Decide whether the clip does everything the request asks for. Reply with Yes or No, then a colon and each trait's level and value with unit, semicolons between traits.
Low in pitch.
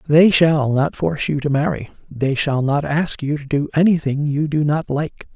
No: medium, 150 Hz